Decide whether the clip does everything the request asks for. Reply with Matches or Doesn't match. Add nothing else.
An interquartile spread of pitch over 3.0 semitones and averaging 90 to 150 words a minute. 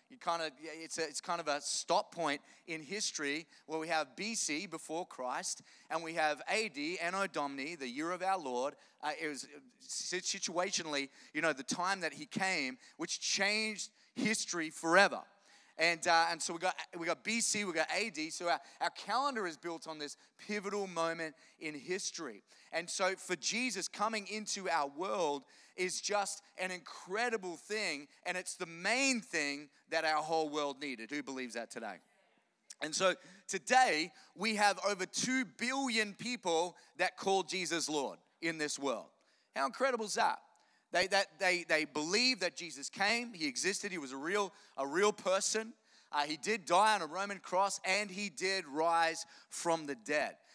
Doesn't match